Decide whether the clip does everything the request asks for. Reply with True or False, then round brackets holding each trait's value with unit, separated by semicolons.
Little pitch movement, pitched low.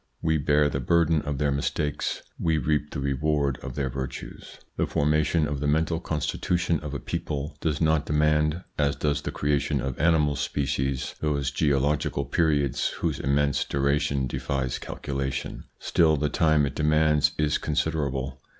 True (1.8 semitones; 75 Hz)